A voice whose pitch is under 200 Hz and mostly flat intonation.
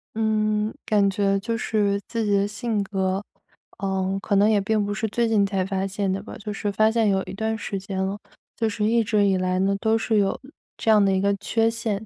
No: high, 205 Hz; narrow, 1.9 semitones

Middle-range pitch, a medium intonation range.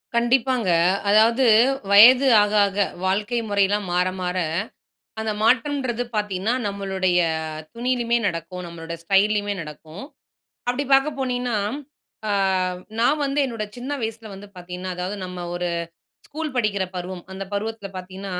No: high, 205 Hz; average, 4.4 semitones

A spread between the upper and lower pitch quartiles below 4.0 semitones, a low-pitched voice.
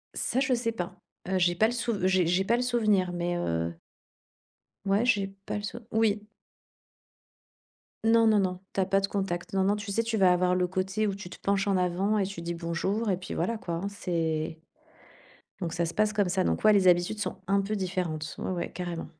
No: average, 3.1 semitones; high, 190 Hz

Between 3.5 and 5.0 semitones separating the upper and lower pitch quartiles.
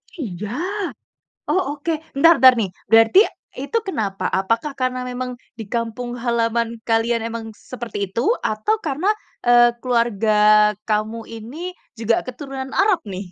No: narrow, 2.5 semitones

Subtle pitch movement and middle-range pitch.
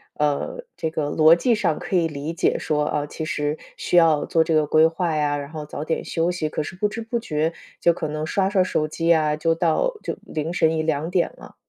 Yes: narrow, 2.1 semitones; medium, 160 Hz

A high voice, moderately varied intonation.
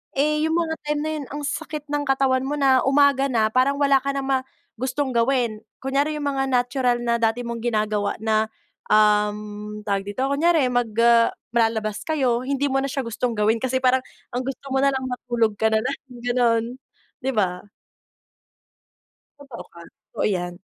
Yes: very high, 255 Hz; average, 3.7 semitones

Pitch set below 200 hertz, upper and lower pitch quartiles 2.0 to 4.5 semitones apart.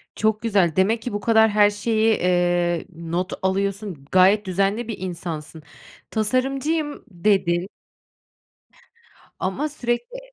No: high, 205 Hz; average, 3.9 semitones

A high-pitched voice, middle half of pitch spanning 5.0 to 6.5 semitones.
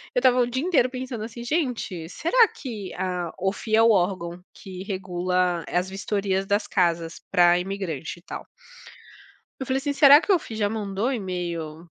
Yes: high, 195 Hz; wide, 5.5 semitones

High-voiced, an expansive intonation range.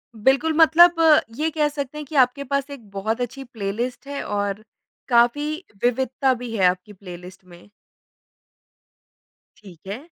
Yes: high, 245 Hz; wide, 5.7 semitones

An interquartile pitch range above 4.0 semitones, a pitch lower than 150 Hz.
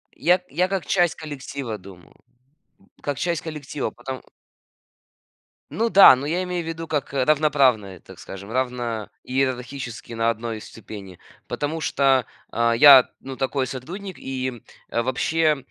Yes: average, 4.8 semitones; low, 135 Hz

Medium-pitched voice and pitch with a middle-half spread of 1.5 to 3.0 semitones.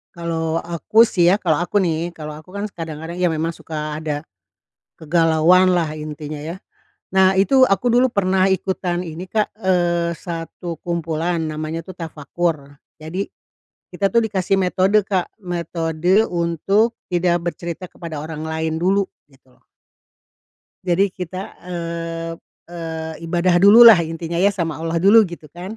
Yes: medium, 170 Hz; narrow, 2.6 semitones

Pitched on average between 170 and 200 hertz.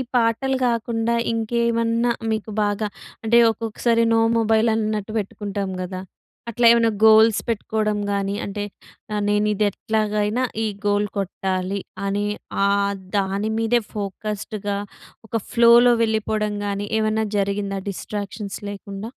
No: high, 215 Hz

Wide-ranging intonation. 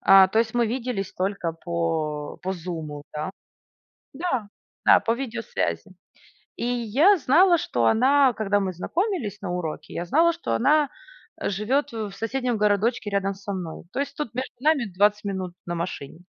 Yes: wide, 6.2 semitones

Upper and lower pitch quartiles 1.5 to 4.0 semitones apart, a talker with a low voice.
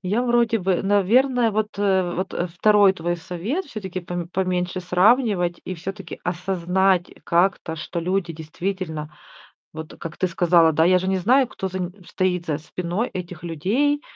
No: average, 2.7 semitones; medium, 185 Hz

